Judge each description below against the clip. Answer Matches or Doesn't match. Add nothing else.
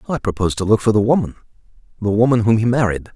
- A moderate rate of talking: Doesn't match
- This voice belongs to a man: Matches